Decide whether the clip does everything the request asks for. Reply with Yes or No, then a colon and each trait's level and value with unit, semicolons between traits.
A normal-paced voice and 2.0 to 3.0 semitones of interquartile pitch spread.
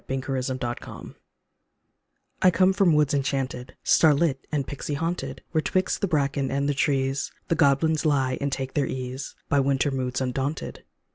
Yes: average, 160 wpm; narrow, 2.5 semitones